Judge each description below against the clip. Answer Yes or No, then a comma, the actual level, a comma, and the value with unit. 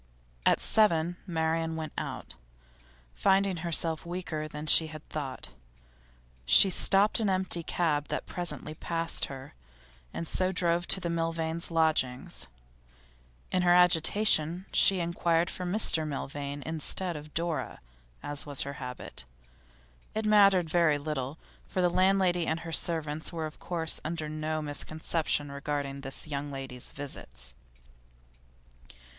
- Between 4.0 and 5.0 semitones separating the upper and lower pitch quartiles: No, average, 3.0 semitones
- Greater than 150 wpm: No, slow, 135 wpm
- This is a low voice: No, medium, 160 Hz